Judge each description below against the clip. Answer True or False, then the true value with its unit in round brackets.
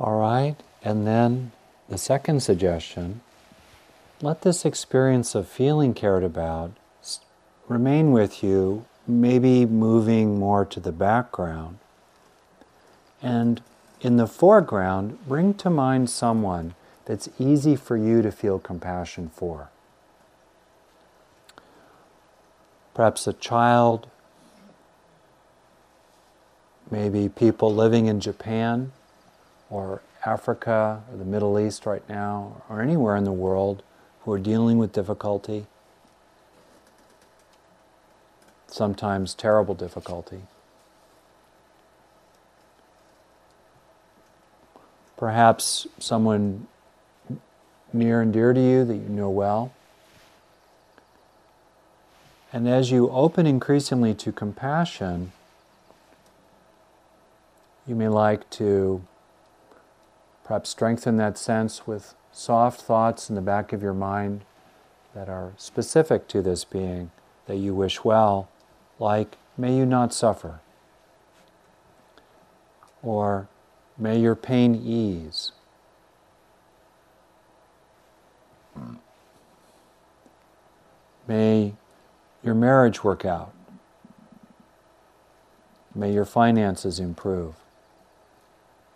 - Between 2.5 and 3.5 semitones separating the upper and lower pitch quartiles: True (3.1 semitones)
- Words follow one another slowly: True (90 wpm)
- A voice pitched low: True (110 Hz)